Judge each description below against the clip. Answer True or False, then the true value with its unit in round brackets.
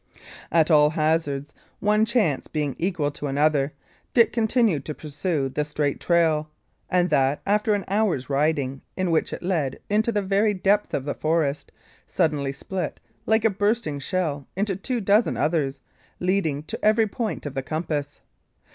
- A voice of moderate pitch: True (160 Hz)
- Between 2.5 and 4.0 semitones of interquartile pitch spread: False (5.6 semitones)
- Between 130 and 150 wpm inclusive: False (160 wpm)